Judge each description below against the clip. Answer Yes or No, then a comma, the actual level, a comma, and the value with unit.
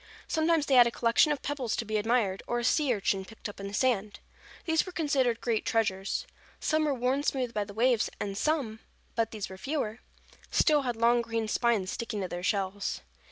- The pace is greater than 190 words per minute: Yes, average, 200 wpm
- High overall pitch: Yes, high, 235 Hz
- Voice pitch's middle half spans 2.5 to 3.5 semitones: No, average, 4.4 semitones